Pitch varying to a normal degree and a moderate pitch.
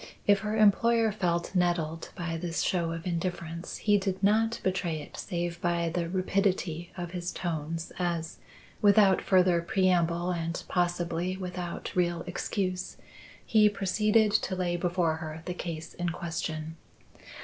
No: narrow, 2.1 semitones; medium, 175 Hz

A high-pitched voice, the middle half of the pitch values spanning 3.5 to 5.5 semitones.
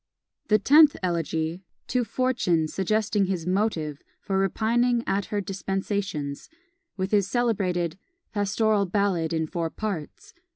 Yes: high, 195 Hz; average, 4.1 semitones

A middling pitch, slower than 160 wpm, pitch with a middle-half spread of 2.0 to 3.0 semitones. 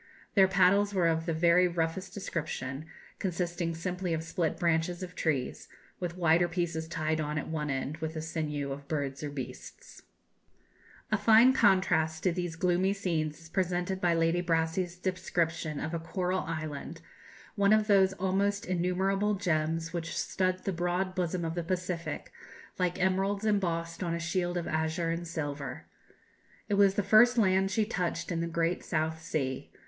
No: medium, 175 Hz; average, 165 wpm; narrow, 2.6 semitones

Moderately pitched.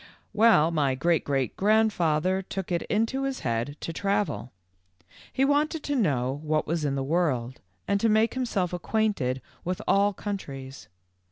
Yes: medium, 180 Hz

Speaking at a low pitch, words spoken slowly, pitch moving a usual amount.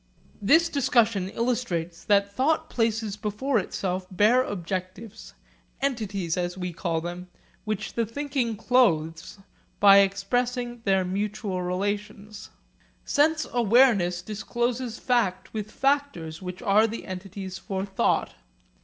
No: high, 205 Hz; slow, 115 wpm; average, 4.4 semitones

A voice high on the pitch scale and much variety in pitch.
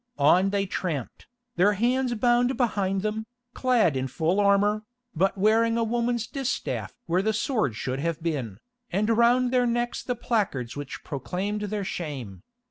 Yes: high, 205 Hz; wide, 5.9 semitones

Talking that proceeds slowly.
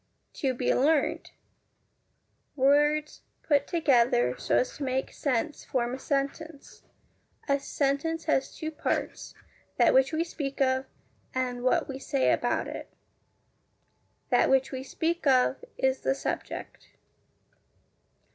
Yes: slow, 125 wpm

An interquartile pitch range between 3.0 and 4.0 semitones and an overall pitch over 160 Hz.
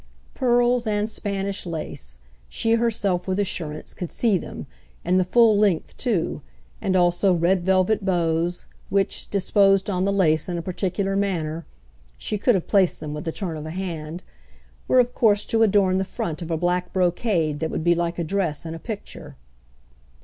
Yes: average, 3.4 semitones; medium, 185 Hz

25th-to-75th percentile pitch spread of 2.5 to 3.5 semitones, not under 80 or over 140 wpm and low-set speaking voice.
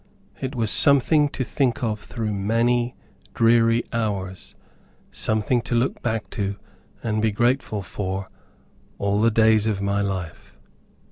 Yes: average, 2.9 semitones; slow, 135 wpm; low, 110 Hz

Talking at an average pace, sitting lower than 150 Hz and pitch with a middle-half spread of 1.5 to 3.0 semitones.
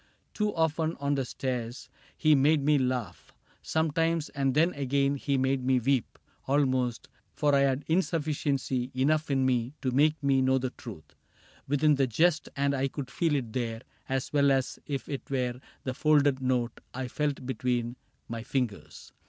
Yes: average, 170 wpm; low, 135 Hz; narrow, 2.5 semitones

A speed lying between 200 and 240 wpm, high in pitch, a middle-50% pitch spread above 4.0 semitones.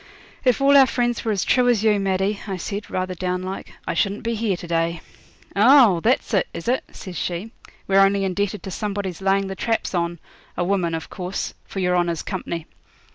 No: fast, 205 wpm; high, 195 Hz; average, 3.2 semitones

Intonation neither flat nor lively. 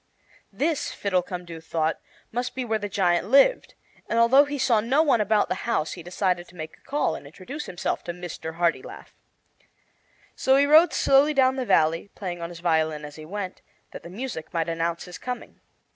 No: wide, 7.4 semitones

